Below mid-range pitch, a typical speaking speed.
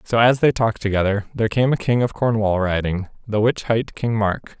No: low, 110 Hz; fast, 220 wpm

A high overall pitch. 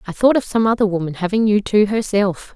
Yes: high, 205 Hz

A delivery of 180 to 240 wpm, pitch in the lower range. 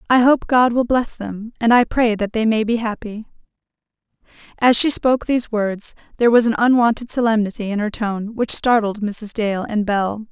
No: average, 190 wpm; high, 225 Hz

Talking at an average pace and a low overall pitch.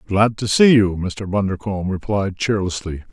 Yes: average, 155 wpm; low, 100 Hz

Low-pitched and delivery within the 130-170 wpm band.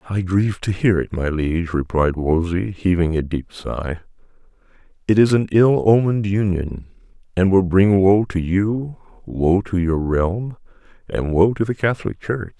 Yes: very low, 95 Hz; average, 165 wpm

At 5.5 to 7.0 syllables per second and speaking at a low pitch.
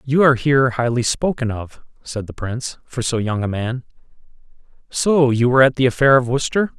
Yes: 5.8 syllables/s; low, 125 Hz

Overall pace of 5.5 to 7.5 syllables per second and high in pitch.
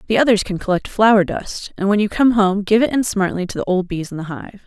Yes: 5.8 syllables/s; high, 200 Hz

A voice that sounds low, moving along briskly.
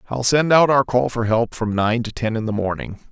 Yes: low, 115 Hz; fast, 270 wpm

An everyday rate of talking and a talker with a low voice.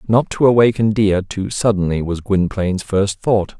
Yes: average, 165 wpm; low, 100 Hz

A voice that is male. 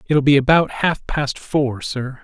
Yes: male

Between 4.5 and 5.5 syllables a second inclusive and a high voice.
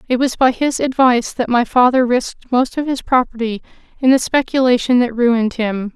Yes: 5.4 syllables/s; high, 245 Hz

